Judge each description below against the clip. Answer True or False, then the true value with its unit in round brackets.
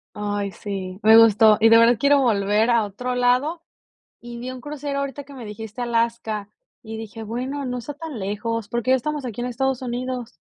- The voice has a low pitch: False (235 Hz)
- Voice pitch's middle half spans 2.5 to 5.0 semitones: True (2.9 semitones)